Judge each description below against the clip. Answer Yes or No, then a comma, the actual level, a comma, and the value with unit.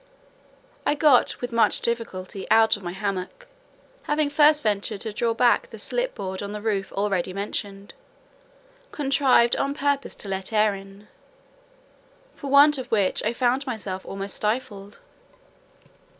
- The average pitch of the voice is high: Yes, high, 220 Hz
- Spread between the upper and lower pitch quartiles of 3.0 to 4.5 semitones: No, wide, 5.6 semitones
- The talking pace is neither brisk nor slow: Yes, average, 145 wpm